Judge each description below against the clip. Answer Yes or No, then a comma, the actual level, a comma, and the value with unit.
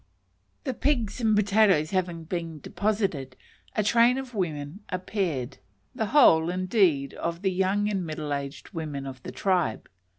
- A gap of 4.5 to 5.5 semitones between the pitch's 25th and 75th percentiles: Yes, average, 5.2 semitones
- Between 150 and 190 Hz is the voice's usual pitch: Yes, medium, 185 Hz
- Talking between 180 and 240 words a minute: No, average, 145 wpm